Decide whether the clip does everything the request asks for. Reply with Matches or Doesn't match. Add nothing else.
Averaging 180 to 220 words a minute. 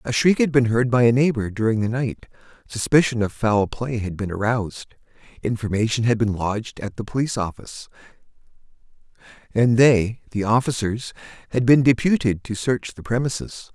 Doesn't match